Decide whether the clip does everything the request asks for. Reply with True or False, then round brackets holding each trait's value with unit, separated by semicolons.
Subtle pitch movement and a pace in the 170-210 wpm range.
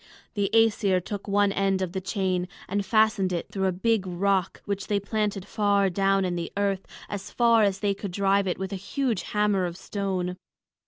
True (1.4 semitones; 200 wpm)